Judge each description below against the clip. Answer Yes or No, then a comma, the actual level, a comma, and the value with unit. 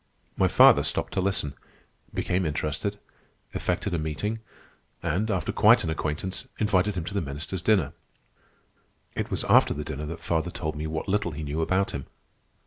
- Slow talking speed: No, average, 170 wpm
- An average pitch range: Yes, average, 3.9 semitones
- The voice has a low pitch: Yes, very low, 85 Hz